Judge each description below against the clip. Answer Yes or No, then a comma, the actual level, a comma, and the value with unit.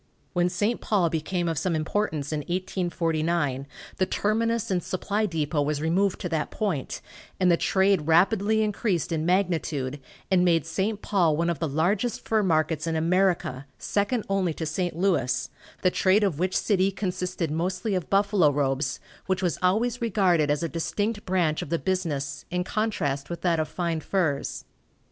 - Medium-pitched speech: Yes, medium, 175 Hz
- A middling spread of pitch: Yes, average, 3.7 semitones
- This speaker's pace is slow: No, average, 170 wpm